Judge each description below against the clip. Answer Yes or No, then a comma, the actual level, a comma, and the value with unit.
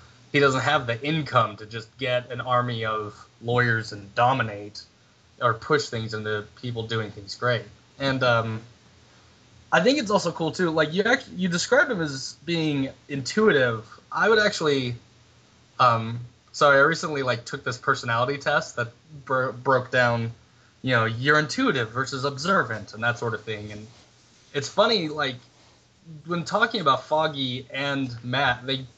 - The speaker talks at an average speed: Yes, average, 160 wpm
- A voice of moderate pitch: No, low, 125 Hz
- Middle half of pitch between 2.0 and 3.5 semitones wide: No, average, 4.6 semitones